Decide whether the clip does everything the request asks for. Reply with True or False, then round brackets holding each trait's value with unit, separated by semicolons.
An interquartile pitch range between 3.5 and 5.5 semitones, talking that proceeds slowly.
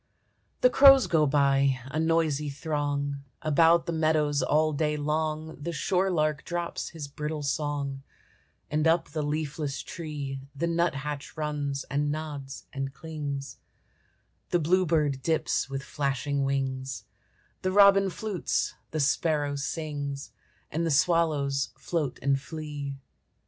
False (2.5 semitones; 130 wpm)